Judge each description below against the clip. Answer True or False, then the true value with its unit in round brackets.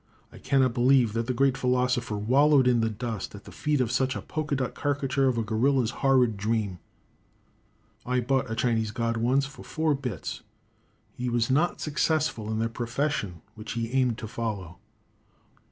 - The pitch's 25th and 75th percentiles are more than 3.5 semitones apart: False (3.1 semitones)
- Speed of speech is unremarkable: True (175 wpm)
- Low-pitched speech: True (125 Hz)